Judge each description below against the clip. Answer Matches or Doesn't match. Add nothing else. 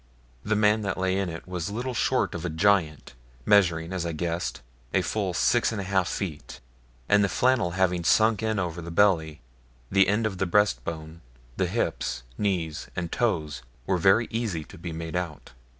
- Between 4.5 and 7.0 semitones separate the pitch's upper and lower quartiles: Doesn't match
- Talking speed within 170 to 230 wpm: Matches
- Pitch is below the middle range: Matches